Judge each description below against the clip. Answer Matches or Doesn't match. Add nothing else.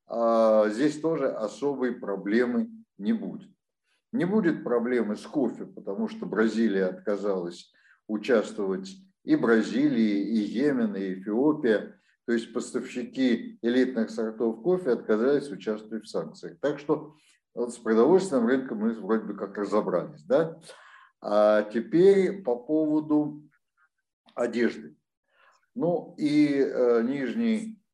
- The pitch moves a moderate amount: Doesn't match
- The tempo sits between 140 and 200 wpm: Doesn't match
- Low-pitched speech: Matches